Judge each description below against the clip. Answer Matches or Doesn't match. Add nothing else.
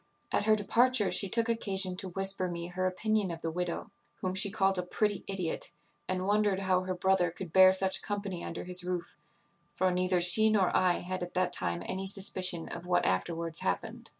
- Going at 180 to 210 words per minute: Matches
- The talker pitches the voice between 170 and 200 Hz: Matches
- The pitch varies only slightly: Matches